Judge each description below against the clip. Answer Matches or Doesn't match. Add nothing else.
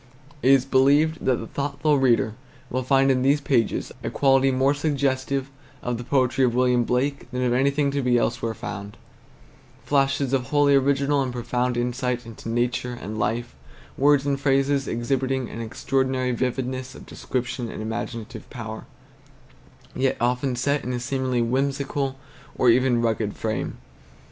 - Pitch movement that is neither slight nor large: Doesn't match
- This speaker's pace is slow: Doesn't match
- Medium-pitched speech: Doesn't match